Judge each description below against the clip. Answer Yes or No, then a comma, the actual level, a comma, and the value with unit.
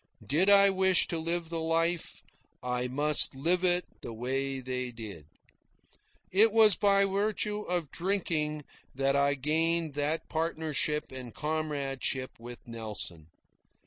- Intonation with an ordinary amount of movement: Yes, average, 5.0 semitones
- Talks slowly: Yes, slow, 130 wpm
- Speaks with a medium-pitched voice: Yes, medium, 155 Hz